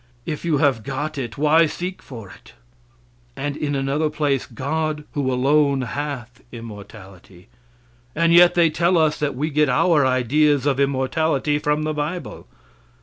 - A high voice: No, medium, 145 Hz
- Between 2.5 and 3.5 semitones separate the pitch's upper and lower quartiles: Yes, average, 2.9 semitones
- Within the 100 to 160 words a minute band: Yes, average, 150 wpm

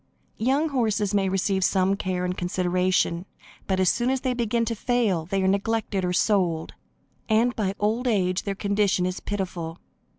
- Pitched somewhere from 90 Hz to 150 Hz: No, high, 195 Hz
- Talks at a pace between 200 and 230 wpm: No, average, 170 wpm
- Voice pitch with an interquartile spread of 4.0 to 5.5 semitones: No, average, 3.5 semitones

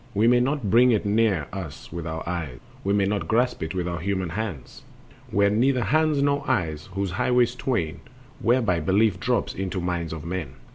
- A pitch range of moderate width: No, wide, 5.8 semitones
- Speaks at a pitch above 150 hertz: No, low, 100 Hz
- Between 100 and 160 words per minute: No, average, 190 wpm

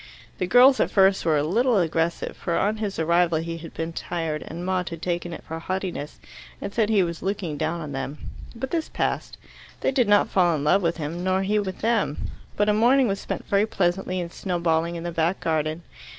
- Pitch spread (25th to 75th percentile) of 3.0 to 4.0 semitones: Yes, average, 3.5 semitones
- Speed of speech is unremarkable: No, fast, 220 wpm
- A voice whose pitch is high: No, medium, 175 Hz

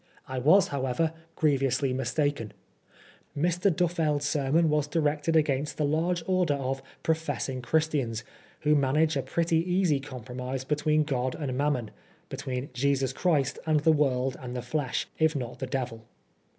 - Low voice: No, medium, 145 Hz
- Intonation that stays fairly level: No, average, 3.3 semitones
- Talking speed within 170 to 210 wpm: No, average, 150 wpm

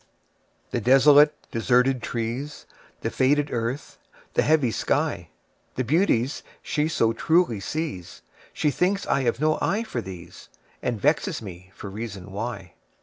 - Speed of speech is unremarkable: No, slow, 120 wpm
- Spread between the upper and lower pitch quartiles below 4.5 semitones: No, average, 4.9 semitones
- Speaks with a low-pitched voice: Yes, low, 125 Hz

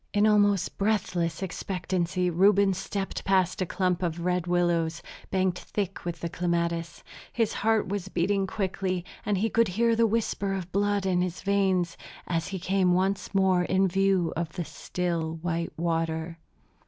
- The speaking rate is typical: Yes, average, 160 wpm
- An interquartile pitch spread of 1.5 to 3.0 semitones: Yes, narrow, 2.4 semitones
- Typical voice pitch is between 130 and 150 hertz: No, medium, 185 Hz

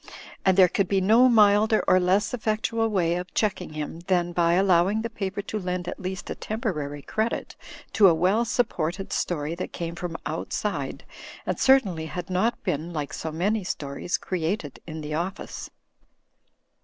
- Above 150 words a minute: Yes, average, 170 wpm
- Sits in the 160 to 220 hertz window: Yes, medium, 185 Hz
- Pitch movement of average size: Yes, average, 3.9 semitones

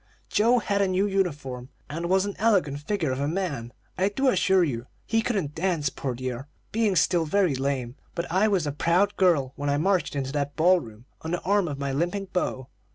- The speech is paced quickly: Yes, fast, 215 wpm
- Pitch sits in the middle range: Yes, medium, 170 Hz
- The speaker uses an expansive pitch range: Yes, wide, 5.7 semitones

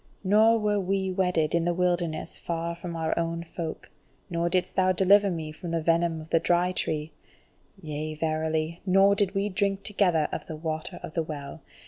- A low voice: No, medium, 170 Hz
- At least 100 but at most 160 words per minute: No, average, 185 wpm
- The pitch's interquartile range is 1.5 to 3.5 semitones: Yes, average, 2.9 semitones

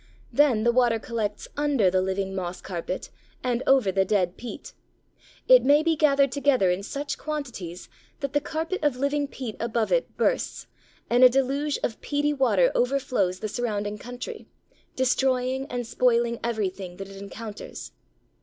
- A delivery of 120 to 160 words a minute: Yes, average, 155 wpm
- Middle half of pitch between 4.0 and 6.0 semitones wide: Yes, wide, 5.4 semitones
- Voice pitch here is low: No, high, 245 Hz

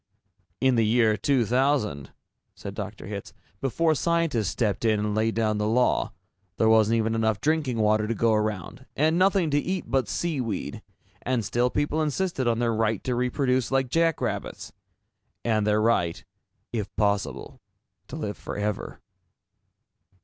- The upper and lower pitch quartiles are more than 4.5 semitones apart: No, average, 4.0 semitones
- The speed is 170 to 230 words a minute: No, average, 150 wpm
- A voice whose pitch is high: No, low, 115 Hz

